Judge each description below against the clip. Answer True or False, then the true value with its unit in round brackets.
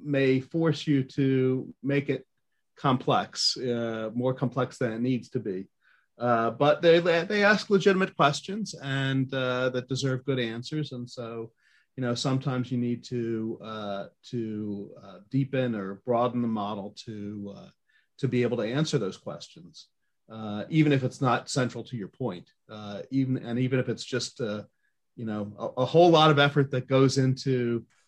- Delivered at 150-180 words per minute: True (175 wpm)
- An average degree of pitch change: True (3.1 semitones)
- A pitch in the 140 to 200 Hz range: False (130 Hz)